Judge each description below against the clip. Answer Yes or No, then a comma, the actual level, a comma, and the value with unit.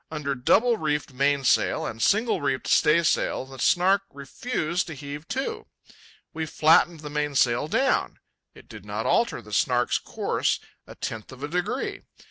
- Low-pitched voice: No, medium, 150 Hz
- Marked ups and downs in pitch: No, average, 4.6 semitones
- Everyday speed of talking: Yes, average, 150 wpm